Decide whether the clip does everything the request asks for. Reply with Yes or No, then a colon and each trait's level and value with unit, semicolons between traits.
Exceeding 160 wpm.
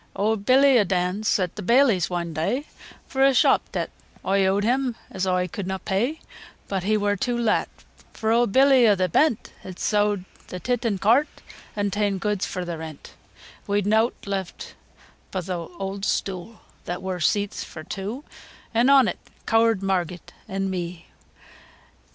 Yes: average, 175 wpm